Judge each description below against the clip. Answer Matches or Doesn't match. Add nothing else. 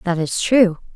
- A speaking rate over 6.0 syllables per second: Doesn't match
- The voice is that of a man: Doesn't match